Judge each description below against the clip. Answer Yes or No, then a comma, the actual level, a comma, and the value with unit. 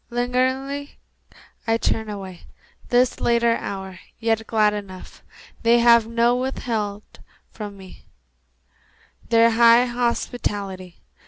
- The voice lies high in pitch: Yes, high, 230 Hz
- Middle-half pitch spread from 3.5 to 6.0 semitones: No, average, 2.8 semitones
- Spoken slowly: Yes, slow, 100 wpm